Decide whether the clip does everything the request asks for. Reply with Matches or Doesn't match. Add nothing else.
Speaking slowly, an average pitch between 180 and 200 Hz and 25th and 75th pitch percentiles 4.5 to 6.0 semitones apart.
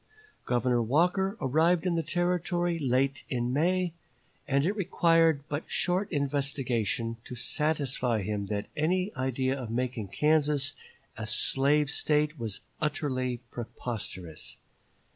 Doesn't match